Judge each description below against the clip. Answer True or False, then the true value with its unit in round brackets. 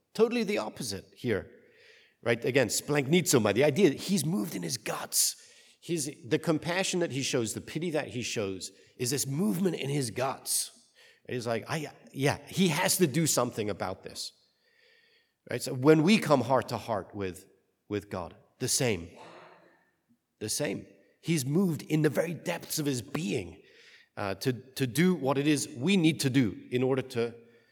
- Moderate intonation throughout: False (6.4 semitones)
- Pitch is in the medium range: True (145 Hz)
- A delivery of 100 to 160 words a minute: False (175 wpm)